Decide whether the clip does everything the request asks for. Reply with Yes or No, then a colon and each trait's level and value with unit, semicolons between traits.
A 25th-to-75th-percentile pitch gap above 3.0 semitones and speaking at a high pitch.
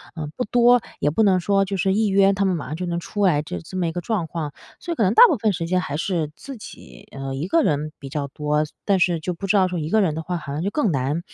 No: average, 4.7 semitones; medium, 175 Hz